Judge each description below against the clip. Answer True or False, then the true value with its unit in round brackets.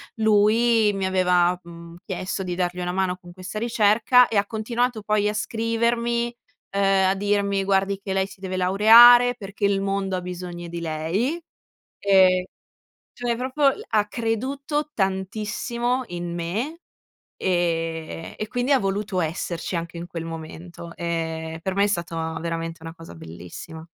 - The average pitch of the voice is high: True (195 Hz)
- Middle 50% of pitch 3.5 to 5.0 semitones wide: True (4.5 semitones)